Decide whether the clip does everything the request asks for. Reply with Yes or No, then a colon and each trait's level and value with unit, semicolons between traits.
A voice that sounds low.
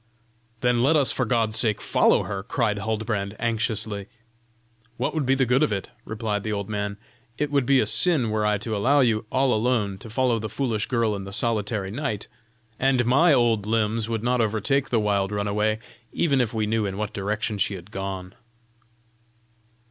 Yes: low, 110 Hz